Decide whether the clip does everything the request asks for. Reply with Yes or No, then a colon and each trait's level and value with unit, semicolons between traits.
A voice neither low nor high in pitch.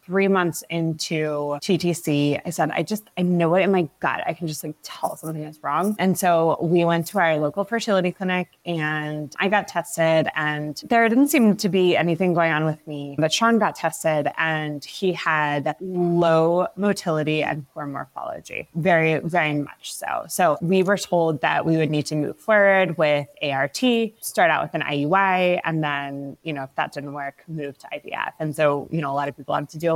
Yes: medium, 165 Hz